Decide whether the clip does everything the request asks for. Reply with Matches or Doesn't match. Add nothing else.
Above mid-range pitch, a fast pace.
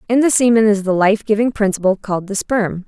Matches